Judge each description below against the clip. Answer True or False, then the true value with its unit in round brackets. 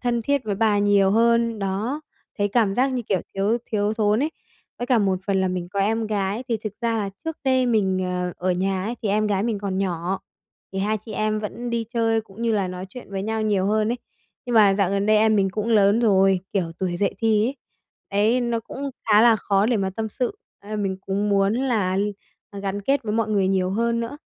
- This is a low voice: False (210 Hz)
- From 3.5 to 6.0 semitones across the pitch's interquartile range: False (2.8 semitones)